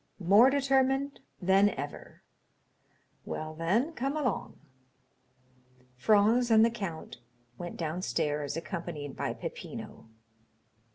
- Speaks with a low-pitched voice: No, high, 200 Hz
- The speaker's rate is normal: No, slow, 95 wpm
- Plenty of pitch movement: Yes, wide, 8.0 semitones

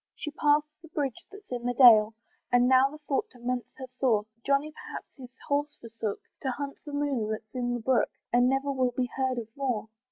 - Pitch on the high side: Yes, very high, 255 Hz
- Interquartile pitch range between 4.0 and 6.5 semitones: No, average, 2.8 semitones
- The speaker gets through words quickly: Yes, fast, 210 wpm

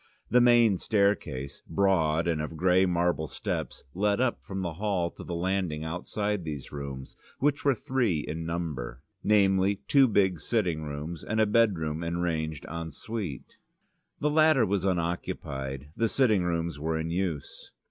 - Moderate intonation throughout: Yes, average, 4.6 semitones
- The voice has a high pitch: No, very low, 90 Hz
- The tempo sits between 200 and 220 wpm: No, average, 155 wpm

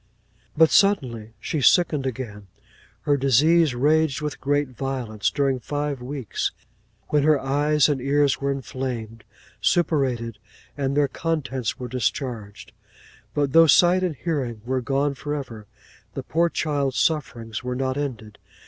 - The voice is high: No, low, 135 Hz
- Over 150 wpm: No, average, 140 wpm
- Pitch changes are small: No, average, 3.1 semitones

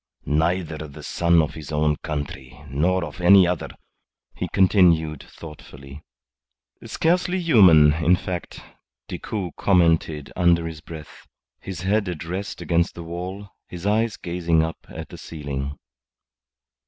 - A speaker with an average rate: No, slow, 130 wpm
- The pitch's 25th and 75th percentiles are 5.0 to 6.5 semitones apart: No, average, 3.2 semitones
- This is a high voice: No, very low, 85 Hz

